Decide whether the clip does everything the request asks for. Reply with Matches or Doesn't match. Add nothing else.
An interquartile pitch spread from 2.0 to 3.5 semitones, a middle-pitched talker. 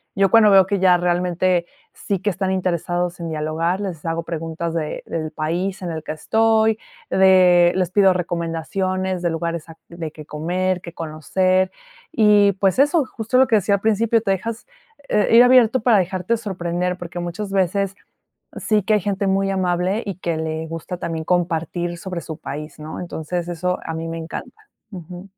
Matches